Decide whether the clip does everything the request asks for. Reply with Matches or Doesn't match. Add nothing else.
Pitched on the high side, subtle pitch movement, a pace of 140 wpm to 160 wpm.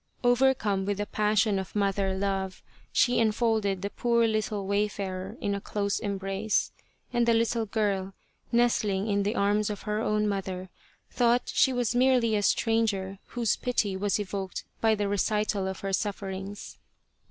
Matches